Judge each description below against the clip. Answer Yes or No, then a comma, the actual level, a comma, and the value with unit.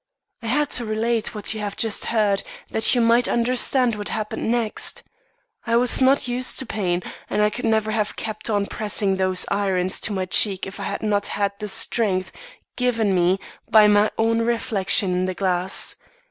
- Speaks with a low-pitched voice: No, high, 215 Hz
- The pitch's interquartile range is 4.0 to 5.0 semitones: No, average, 2.8 semitones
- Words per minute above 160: Yes, average, 190 wpm